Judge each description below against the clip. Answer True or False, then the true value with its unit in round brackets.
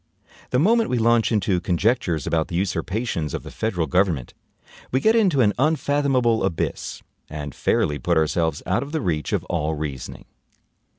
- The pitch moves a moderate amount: False (8.1 semitones)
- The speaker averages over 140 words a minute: True (165 wpm)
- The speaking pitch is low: True (95 Hz)